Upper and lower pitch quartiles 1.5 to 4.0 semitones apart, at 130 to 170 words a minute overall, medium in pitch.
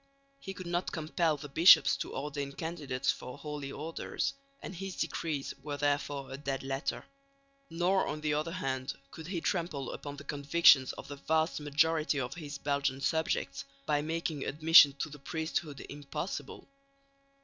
Yes: average, 2.7 semitones; average, 160 wpm; medium, 150 Hz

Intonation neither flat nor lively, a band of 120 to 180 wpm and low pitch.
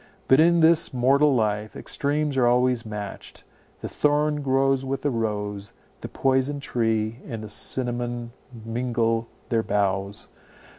Yes: average, 3.6 semitones; slow, 135 wpm; low, 120 Hz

